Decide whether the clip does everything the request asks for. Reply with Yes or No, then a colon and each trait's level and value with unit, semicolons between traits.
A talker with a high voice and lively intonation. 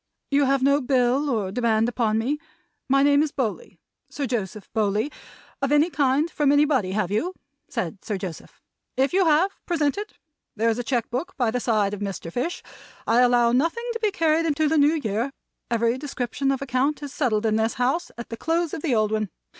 No: very high, 255 Hz; average, 4.8 semitones